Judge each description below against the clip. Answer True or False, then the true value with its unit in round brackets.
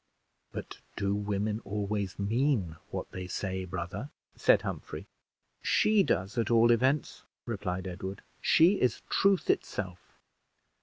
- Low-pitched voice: True (105 Hz)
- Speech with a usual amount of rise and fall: True (4.1 semitones)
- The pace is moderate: False (120 wpm)